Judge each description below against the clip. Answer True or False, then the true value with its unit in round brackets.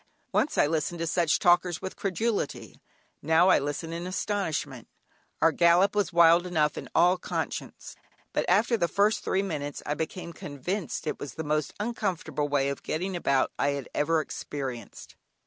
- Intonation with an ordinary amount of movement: True (3.9 semitones)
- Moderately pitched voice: True (165 Hz)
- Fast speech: False (165 wpm)